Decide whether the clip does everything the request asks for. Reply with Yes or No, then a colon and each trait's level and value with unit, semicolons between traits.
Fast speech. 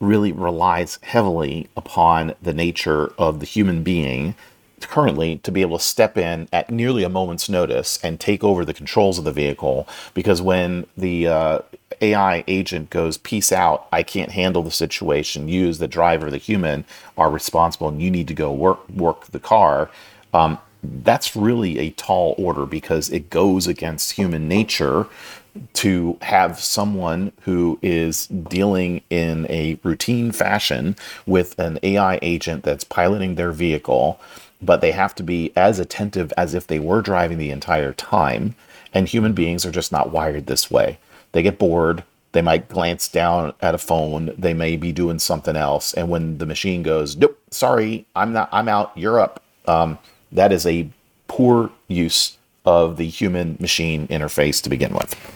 No: average, 170 wpm